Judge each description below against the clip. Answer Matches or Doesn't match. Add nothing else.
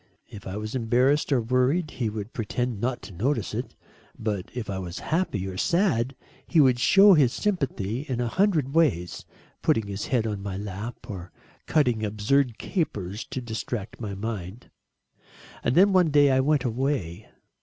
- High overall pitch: Doesn't match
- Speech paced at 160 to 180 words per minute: Matches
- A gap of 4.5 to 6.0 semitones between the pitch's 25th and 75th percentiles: Matches